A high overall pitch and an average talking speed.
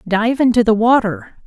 Yes: high, 225 Hz; average, 165 wpm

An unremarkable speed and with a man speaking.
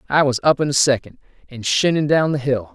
No: fast, 240 wpm; male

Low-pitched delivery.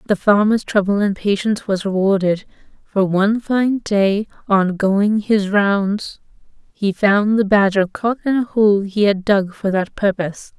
No: high, 205 Hz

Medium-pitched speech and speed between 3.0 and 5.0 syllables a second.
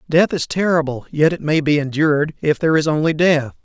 No: medium, 155 Hz; 5.8 syllables/s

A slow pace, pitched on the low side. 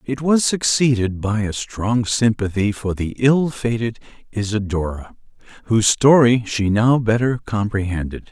Yes: slow, 130 wpm; low, 110 Hz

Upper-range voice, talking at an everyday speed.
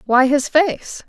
Yes: very high, 280 Hz; average, 165 wpm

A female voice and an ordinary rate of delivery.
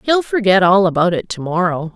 No: female; fast, 215 wpm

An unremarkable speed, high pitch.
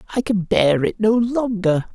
Yes: average, 185 wpm; high, 205 Hz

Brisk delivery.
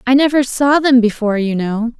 Yes: fast, 210 wpm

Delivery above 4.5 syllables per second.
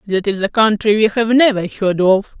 Yes: 5.0 syllables/s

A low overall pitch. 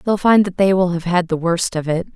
No: medium, 180 Hz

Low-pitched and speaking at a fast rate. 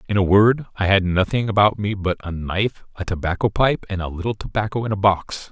Yes: low, 100 Hz; fast, 230 wpm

